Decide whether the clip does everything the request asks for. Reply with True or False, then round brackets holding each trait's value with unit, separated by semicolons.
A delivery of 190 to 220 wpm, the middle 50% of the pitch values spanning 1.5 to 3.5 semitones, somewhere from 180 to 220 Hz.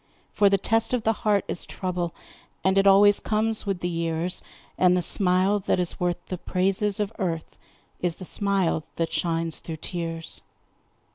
False (170 wpm; 2.7 semitones; 185 Hz)